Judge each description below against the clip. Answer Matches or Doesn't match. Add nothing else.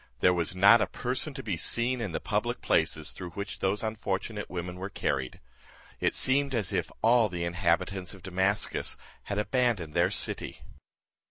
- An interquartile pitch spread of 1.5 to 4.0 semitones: Doesn't match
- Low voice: Matches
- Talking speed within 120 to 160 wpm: Doesn't match